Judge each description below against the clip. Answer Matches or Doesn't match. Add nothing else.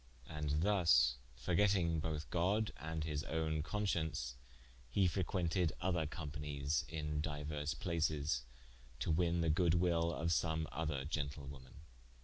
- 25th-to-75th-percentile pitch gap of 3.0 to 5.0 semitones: Doesn't match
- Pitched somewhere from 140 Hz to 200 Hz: Doesn't match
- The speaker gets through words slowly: Matches